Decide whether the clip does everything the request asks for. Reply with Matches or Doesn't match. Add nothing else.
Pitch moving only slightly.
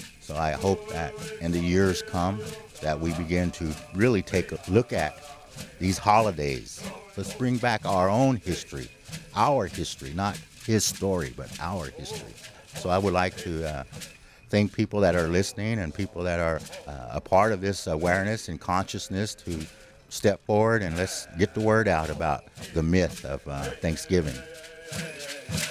Doesn't match